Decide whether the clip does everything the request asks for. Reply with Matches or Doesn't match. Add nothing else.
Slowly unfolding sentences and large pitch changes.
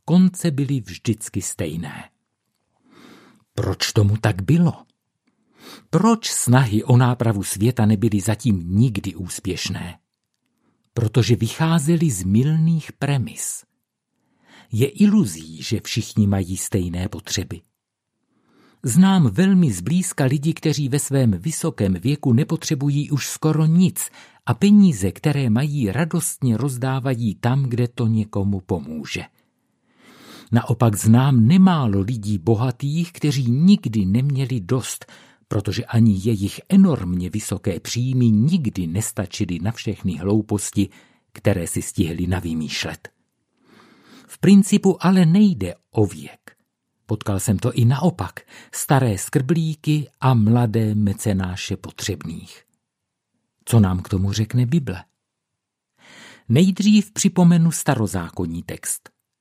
Matches